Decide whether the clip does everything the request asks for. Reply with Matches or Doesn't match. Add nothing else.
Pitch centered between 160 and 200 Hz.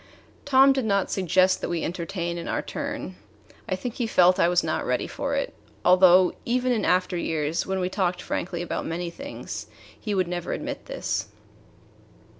Matches